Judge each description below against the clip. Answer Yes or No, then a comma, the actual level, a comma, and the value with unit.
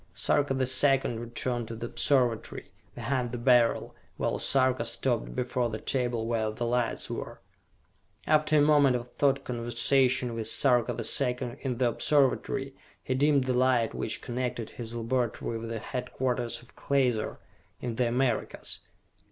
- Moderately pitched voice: No, low, 125 Hz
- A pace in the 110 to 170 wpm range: Yes, average, 150 wpm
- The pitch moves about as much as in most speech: No, narrow, 1.9 semitones